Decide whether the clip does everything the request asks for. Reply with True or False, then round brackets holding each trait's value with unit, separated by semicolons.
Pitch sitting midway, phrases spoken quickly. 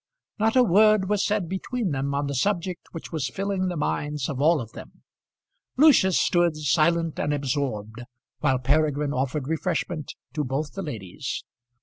False (155 Hz; 160 wpm)